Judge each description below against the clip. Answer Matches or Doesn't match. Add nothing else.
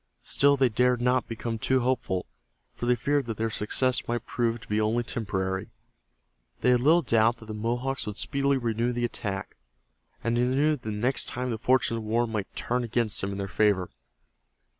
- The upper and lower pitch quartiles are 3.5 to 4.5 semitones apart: Doesn't match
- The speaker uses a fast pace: Doesn't match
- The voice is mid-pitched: Doesn't match